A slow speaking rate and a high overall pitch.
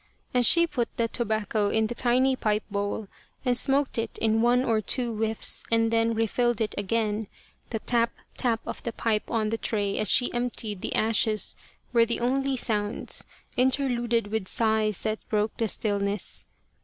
No: average, 170 wpm; high, 225 Hz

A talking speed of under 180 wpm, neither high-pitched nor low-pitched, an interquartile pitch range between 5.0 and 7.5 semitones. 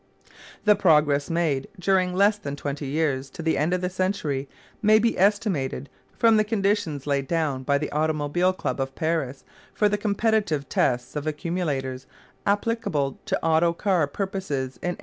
Yes: average, 165 wpm; medium, 160 Hz; wide, 5.6 semitones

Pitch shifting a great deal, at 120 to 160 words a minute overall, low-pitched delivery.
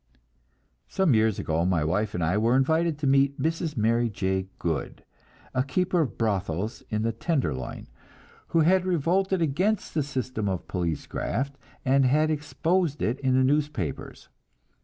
Yes: wide, 7.0 semitones; average, 155 wpm; low, 130 Hz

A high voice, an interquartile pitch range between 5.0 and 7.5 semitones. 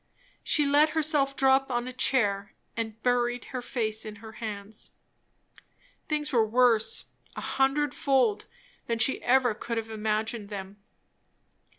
No: high, 240 Hz; average, 3.6 semitones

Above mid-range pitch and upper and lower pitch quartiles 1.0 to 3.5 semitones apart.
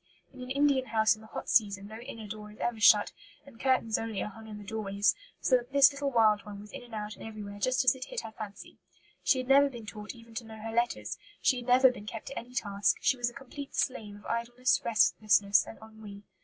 Yes: high, 225 Hz; average, 3.2 semitones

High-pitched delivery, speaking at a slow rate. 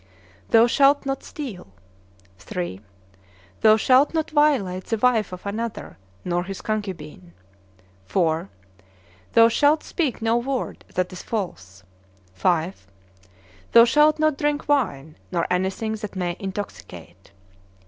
Yes: high, 210 Hz; slow, 120 wpm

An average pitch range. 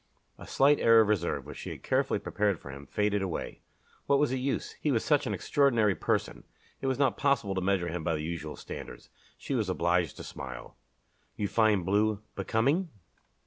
No: wide, 6.8 semitones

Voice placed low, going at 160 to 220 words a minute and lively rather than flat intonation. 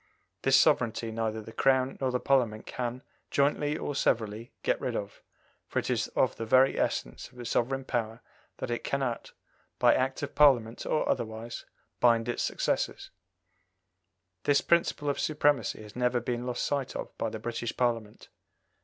No: low, 120 Hz; average, 165 wpm; average, 2.9 semitones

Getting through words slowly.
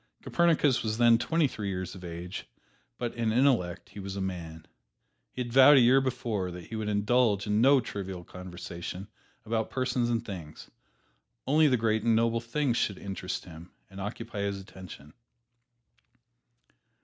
No: average, 160 wpm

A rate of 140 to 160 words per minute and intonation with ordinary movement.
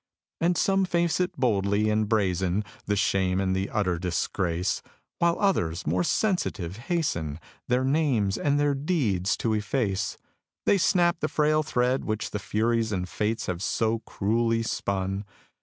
No: average, 150 wpm; wide, 7.1 semitones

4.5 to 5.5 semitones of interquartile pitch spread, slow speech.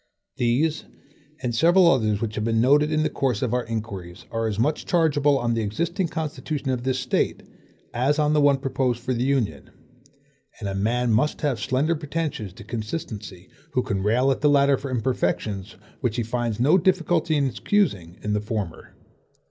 No: average, 5.1 semitones; average, 185 wpm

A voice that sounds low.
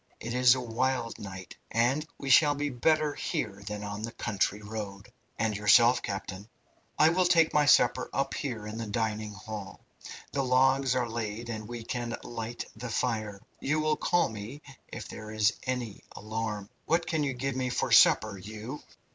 Yes: low, 115 Hz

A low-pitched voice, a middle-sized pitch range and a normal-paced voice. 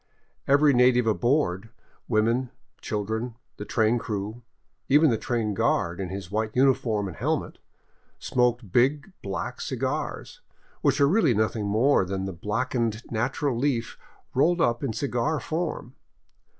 Yes: low, 120 Hz; average, 4.0 semitones; average, 145 wpm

